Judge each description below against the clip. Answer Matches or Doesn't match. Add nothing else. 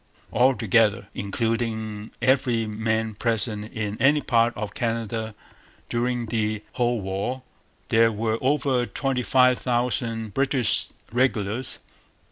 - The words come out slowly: Matches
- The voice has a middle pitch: Doesn't match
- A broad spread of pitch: Doesn't match